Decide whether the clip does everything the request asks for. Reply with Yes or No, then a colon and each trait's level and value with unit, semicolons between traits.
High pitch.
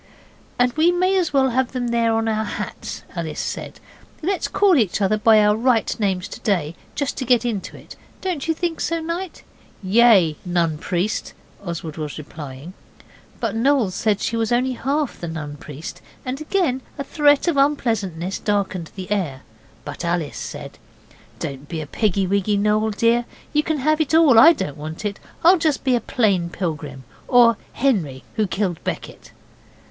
Yes: high, 220 Hz